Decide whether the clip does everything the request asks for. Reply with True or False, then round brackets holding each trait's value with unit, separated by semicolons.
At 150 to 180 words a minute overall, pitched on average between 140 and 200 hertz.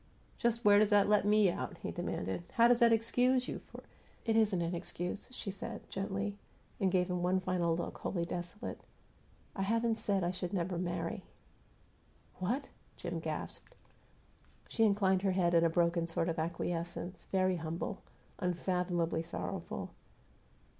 True (160 wpm; 185 Hz)